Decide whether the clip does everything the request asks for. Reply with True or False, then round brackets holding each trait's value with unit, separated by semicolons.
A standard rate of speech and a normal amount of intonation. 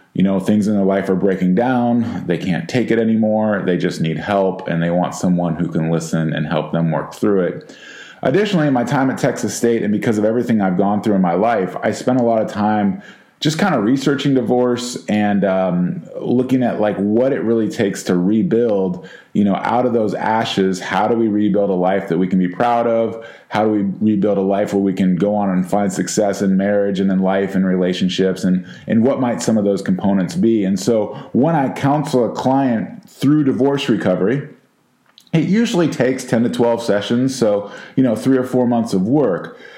False (215 wpm; 4.1 semitones)